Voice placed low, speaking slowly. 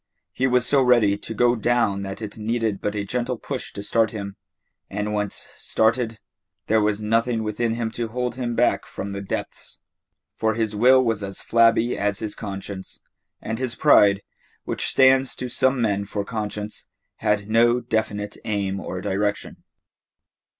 No: low, 110 Hz; average, 165 wpm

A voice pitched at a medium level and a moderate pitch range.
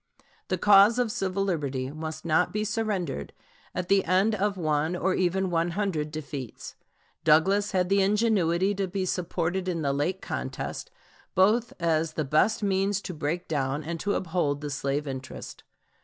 Yes: medium, 180 Hz; average, 4.2 semitones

